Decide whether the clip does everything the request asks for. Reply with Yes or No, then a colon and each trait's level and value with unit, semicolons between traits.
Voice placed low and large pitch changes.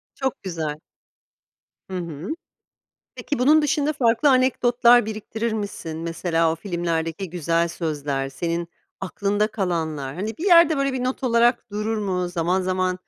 No: high, 190 Hz; wide, 6.2 semitones